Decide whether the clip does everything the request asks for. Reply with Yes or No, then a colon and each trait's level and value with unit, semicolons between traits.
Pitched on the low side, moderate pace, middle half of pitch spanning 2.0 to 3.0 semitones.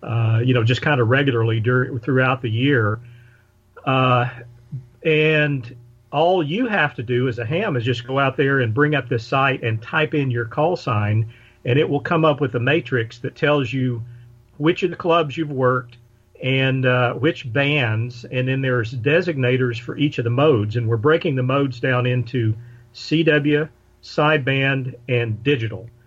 No: low, 130 Hz; average, 180 wpm; average, 3.7 semitones